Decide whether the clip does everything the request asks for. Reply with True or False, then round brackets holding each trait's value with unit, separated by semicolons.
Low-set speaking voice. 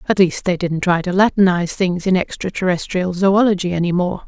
False (185 Hz)